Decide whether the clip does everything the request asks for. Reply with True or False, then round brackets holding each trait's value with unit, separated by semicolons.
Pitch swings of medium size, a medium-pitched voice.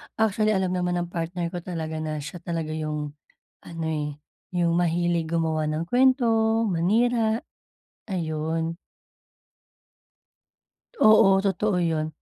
True (3.2 semitones; 170 Hz)